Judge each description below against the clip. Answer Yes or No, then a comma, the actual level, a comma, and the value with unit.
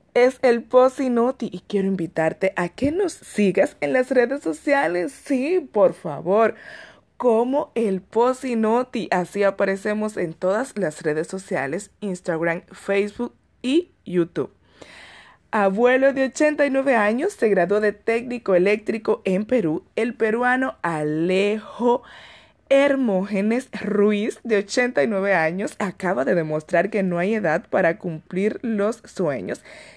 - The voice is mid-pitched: No, high, 210 Hz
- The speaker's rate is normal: No, slow, 120 wpm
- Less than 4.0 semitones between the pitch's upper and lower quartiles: No, average, 4.7 semitones